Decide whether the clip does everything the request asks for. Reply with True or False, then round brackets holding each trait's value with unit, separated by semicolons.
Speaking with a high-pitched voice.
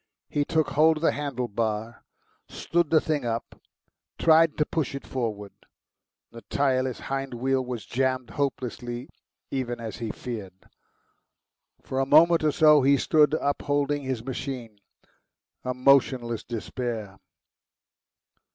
False (130 Hz)